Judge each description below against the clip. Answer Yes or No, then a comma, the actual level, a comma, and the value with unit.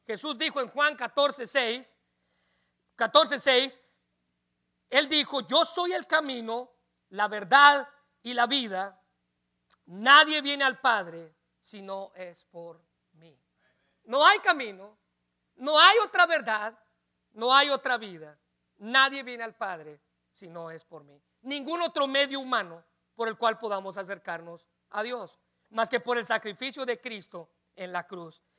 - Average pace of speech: Yes, average, 140 wpm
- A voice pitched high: Yes, high, 225 Hz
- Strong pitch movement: Yes, wide, 8.1 semitones